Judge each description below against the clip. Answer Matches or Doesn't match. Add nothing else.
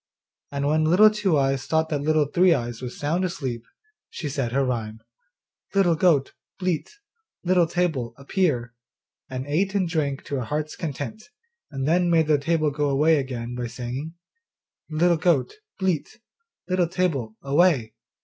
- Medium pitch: Matches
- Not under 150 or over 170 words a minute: Matches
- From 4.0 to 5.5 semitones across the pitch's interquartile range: Matches